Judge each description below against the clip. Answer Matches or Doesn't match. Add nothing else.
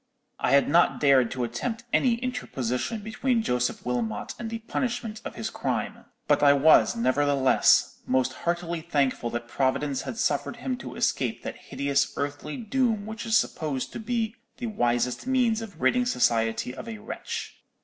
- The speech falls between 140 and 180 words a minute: Matches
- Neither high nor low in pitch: Matches